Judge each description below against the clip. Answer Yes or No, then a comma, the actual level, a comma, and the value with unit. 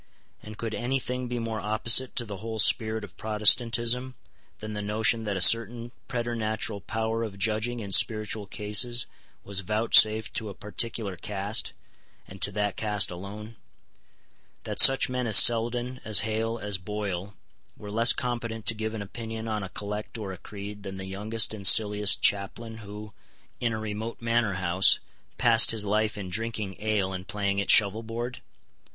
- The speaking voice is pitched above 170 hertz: No, low, 110 Hz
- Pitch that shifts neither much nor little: No, narrow, 2.0 semitones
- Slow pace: No, average, 170 wpm